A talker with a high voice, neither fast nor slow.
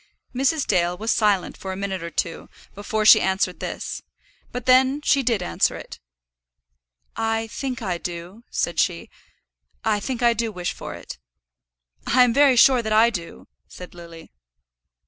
Yes: high, 215 Hz; average, 165 wpm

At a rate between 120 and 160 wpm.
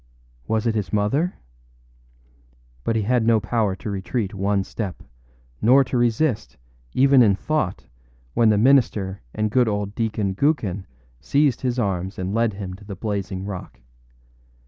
Yes: average, 150 wpm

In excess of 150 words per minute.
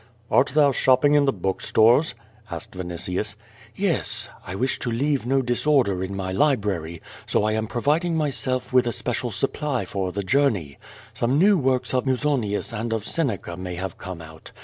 Yes: average, 175 wpm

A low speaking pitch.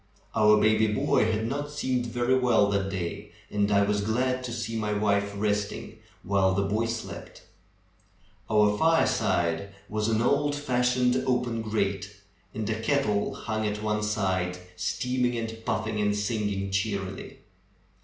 Yes: low, 105 Hz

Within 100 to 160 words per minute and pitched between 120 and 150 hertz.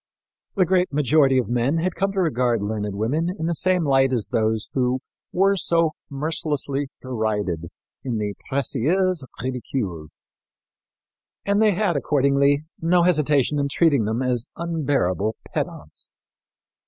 Yes: slow, 135 wpm; medium, 140 Hz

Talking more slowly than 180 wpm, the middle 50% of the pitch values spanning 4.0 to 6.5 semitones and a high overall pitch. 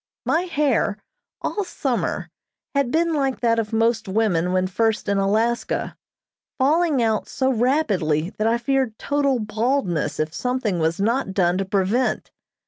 Yes: average, 145 wpm; wide, 5.4 semitones; high, 225 Hz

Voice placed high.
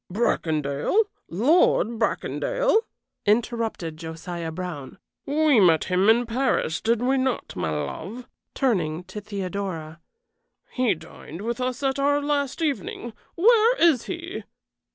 Yes: high, 225 Hz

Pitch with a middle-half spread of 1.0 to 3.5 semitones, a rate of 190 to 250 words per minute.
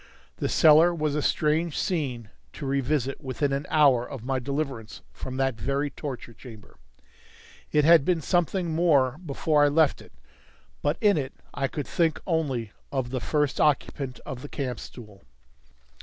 No: average, 3.1 semitones; average, 160 wpm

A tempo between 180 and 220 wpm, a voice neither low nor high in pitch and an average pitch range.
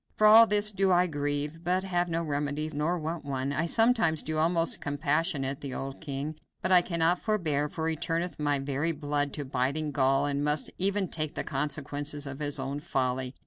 Yes: average, 195 wpm; medium, 150 Hz; average, 3.1 semitones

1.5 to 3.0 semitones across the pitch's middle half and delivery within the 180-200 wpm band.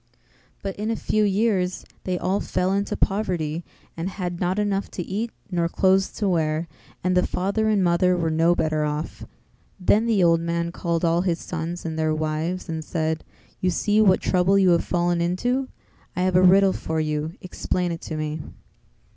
Yes: average, 2.7 semitones; average, 190 wpm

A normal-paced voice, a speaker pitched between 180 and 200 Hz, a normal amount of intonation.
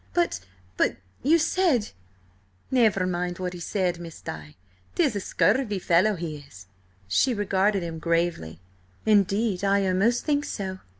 No: slow, 130 wpm; medium, 185 Hz; average, 4.4 semitones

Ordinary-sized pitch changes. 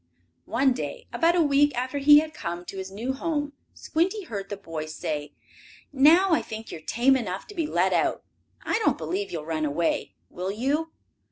No: wide, 8.6 semitones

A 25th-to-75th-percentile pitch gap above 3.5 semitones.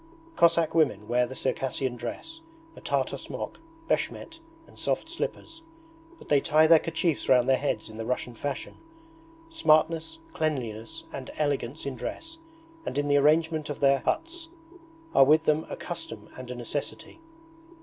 Yes: average, 4.2 semitones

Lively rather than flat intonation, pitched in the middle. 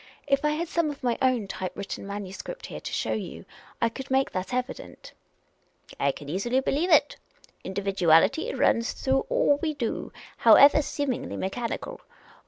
No: wide, 6.5 semitones; very high, 255 Hz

